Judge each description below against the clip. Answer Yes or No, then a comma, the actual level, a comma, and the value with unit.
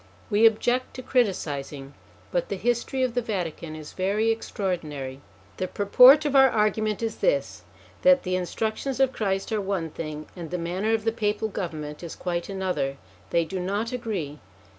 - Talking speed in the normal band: Yes, average, 170 wpm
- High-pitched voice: Yes, high, 200 Hz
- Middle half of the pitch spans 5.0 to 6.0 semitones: Yes, average, 5.3 semitones